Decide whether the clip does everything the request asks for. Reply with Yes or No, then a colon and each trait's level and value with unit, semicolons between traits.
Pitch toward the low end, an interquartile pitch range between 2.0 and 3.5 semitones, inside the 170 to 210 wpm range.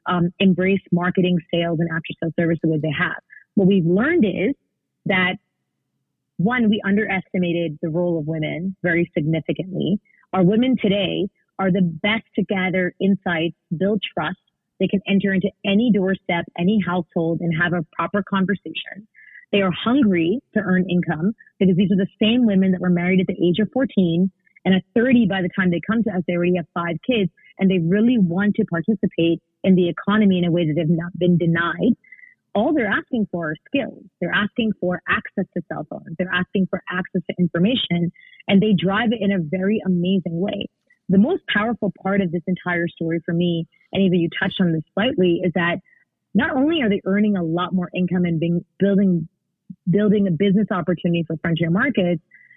No: medium, 185 Hz; average, 2.8 semitones; average, 190 wpm